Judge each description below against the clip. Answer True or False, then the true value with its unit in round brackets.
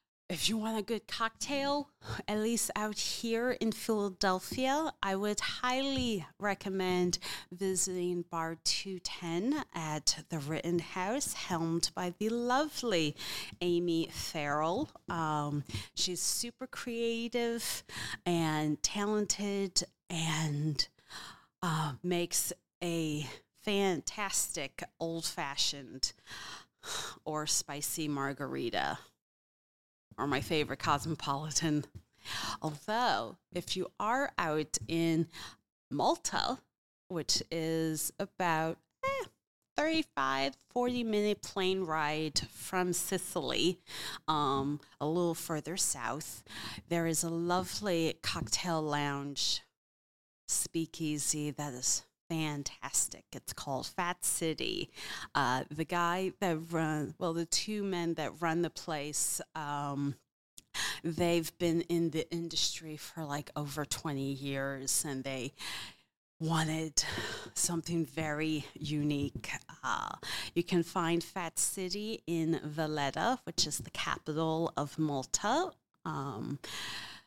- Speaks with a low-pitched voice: False (165 Hz)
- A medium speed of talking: False (100 wpm)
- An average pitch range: True (4.0 semitones)